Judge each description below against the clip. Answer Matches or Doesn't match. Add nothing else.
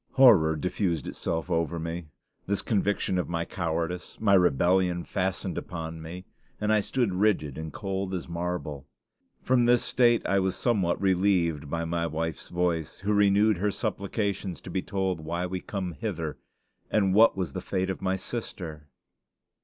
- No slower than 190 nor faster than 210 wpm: Doesn't match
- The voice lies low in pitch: Matches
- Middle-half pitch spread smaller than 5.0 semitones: Matches